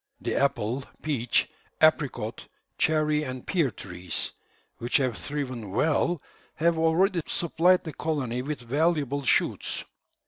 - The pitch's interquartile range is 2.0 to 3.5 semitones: No, average, 4.6 semitones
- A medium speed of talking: No, slow, 115 wpm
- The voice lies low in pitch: No, medium, 145 Hz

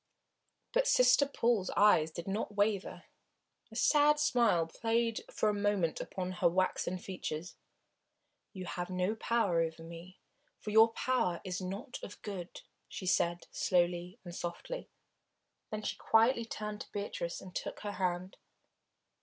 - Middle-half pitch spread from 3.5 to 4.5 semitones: Yes, average, 4.1 semitones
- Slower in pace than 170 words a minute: Yes, average, 145 wpm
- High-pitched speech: Yes, high, 195 Hz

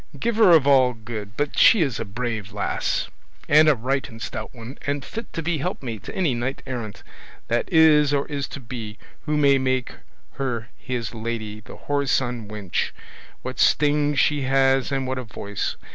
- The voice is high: No, low, 130 Hz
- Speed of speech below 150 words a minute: No, average, 180 wpm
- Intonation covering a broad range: No, average, 3.9 semitones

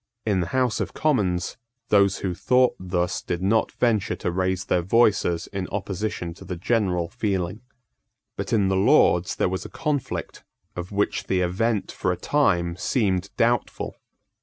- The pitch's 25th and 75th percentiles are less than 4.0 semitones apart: Yes, average, 3.6 semitones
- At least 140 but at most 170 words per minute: Yes, average, 160 wpm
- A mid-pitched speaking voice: No, very low, 95 Hz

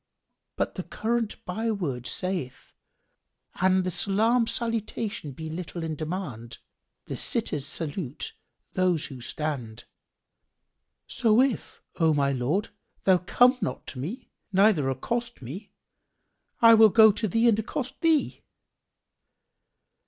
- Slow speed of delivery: Yes, slow, 120 wpm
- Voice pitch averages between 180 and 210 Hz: Yes, medium, 185 Hz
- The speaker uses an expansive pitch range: Yes, wide, 7.3 semitones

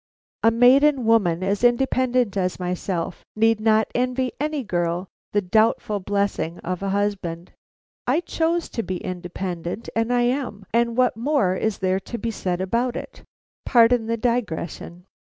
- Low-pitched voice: No, high, 220 Hz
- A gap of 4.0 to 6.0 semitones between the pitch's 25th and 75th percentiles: Yes, average, 4.9 semitones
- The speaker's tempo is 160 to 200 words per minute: No, average, 150 wpm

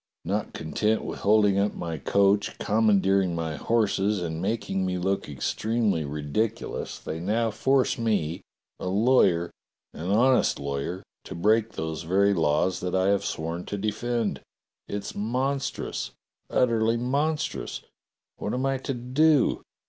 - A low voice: Yes, low, 100 Hz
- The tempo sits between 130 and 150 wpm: Yes, slow, 135 wpm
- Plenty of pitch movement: No, average, 4.6 semitones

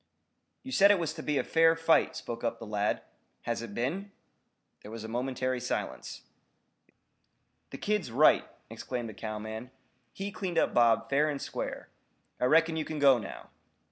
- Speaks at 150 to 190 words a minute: Yes, average, 170 wpm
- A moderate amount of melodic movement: No, wide, 5.9 semitones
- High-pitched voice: No, low, 130 Hz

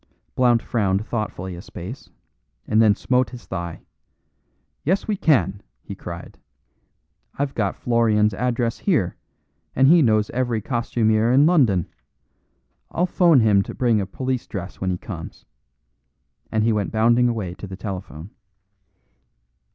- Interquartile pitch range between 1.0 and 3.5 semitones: No, average, 4.1 semitones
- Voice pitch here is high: No, low, 110 Hz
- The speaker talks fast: No, average, 140 wpm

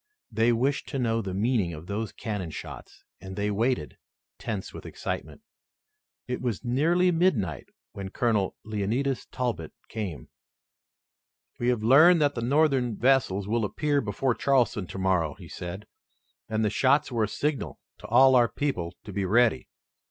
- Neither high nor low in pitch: No, low, 115 Hz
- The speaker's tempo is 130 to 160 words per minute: Yes, average, 155 wpm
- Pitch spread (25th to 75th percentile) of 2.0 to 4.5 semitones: No, average, 4.9 semitones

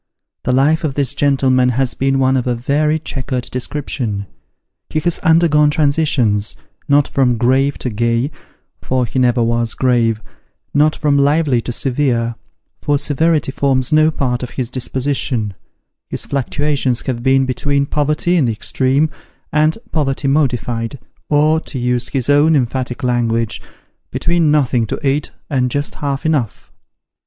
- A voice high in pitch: No, low, 135 Hz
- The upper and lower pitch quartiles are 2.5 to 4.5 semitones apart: Yes, average, 3.1 semitones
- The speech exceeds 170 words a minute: No, average, 150 wpm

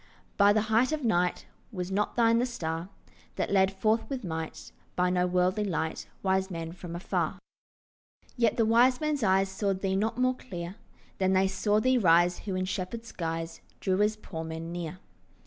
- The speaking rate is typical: Yes, average, 180 wpm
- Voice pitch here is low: No, high, 190 Hz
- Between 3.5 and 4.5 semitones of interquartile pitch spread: Yes, average, 3.9 semitones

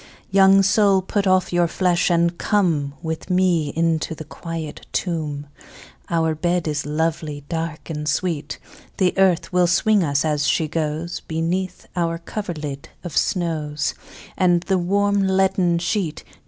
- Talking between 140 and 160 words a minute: Yes, average, 145 wpm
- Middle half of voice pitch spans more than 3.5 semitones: No, average, 3.0 semitones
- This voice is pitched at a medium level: Yes, medium, 170 Hz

